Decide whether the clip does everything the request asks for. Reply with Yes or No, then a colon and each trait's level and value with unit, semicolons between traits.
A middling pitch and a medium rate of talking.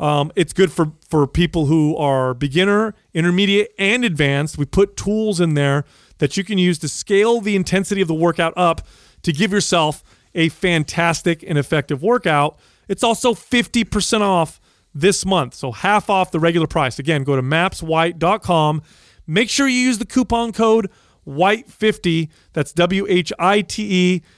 Yes: medium, 175 Hz; average, 155 wpm